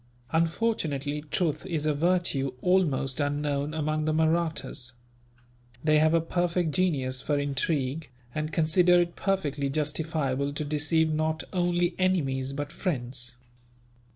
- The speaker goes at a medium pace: No, slow, 125 wpm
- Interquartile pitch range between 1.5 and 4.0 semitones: Yes, average, 3.0 semitones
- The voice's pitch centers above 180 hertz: No, medium, 155 Hz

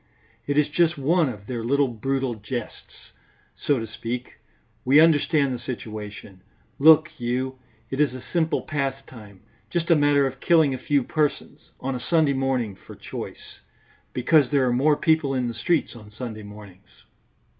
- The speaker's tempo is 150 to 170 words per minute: Yes, average, 165 wpm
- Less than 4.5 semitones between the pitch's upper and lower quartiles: Yes, average, 3.8 semitones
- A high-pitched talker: No, low, 135 Hz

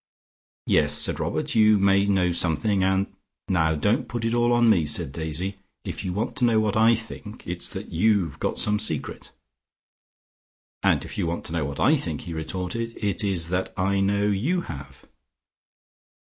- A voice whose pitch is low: Yes, low, 100 Hz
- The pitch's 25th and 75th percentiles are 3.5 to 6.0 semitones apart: Yes, average, 4.3 semitones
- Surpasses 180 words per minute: Yes, average, 190 wpm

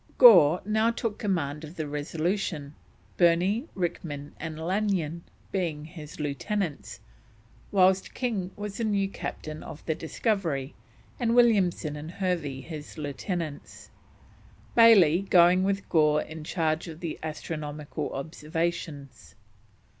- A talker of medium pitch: Yes, medium, 165 Hz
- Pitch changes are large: No, average, 4.4 semitones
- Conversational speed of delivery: No, slow, 115 wpm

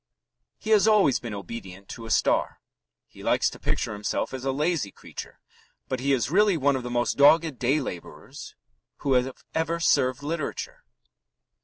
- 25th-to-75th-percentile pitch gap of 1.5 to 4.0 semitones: No, average, 5.1 semitones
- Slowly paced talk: No, average, 170 wpm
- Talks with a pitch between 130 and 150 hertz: Yes, low, 135 Hz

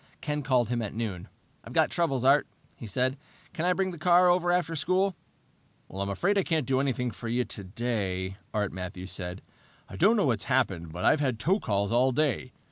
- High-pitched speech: No, low, 125 Hz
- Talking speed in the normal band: No, fast, 210 wpm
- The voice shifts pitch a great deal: Yes, wide, 8.4 semitones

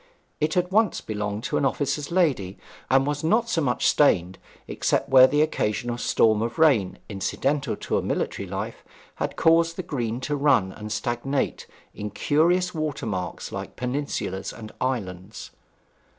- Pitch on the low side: Yes, low, 130 Hz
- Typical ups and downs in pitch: No, wide, 6.3 semitones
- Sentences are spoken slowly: No, average, 150 wpm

